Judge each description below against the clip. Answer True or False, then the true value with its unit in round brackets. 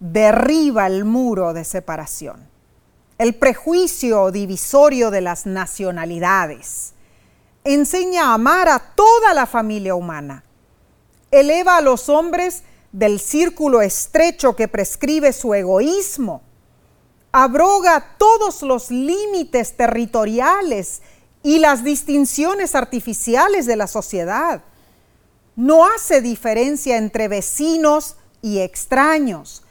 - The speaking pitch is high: True (255 Hz)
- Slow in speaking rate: True (100 wpm)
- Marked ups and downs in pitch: True (7.1 semitones)